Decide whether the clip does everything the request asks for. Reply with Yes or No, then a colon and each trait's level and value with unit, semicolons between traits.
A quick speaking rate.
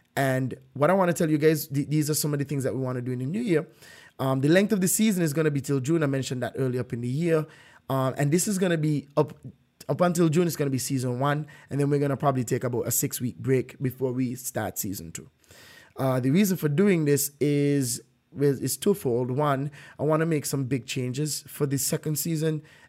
Yes: fast, 245 wpm